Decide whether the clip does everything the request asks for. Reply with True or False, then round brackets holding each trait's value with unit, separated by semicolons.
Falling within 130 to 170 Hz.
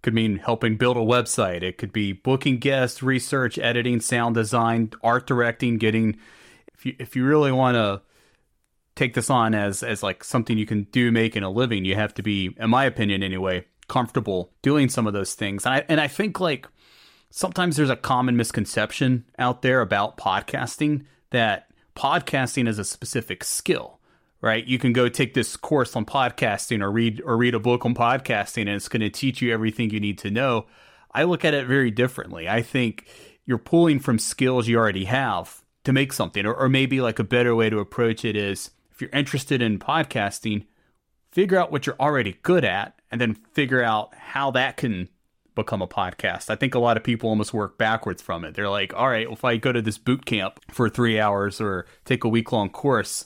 False (120 Hz)